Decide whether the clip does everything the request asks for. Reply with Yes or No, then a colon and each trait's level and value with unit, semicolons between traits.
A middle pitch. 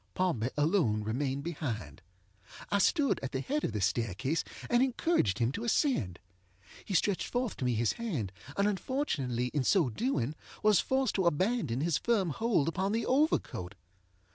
Yes: medium, 165 Hz